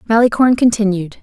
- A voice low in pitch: No, high, 215 Hz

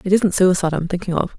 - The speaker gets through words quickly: Yes, fast, 305 wpm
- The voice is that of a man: No, female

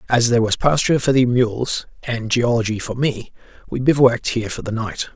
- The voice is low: Yes, low, 120 Hz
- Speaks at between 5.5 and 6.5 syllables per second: Yes, 5.6 syllables/s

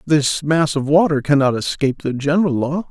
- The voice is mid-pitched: Yes, medium, 145 Hz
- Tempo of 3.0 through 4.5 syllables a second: No, 5.4 syllables/s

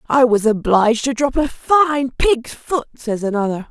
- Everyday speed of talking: Yes, average, 180 wpm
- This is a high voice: Yes, very high, 250 Hz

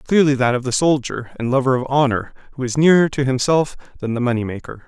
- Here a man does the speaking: Yes, male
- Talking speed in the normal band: No, fast, 220 wpm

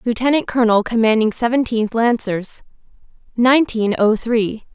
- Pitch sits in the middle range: No, high, 230 Hz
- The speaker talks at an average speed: No, slow, 100 wpm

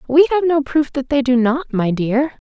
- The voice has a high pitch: Yes, very high, 275 Hz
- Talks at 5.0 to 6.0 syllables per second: No, 4.6 syllables/s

